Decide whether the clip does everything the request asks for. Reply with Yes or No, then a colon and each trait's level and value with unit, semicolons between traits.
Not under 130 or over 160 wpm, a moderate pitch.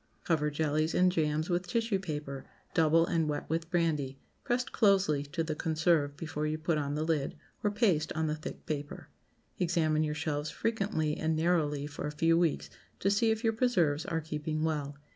No: average, 185 wpm; medium, 160 Hz